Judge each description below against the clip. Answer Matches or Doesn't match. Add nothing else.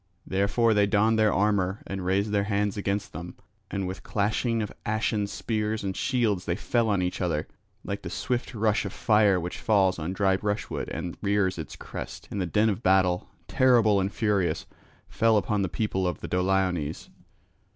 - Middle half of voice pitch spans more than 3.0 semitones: Doesn't match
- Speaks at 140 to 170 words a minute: Doesn't match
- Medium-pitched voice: Doesn't match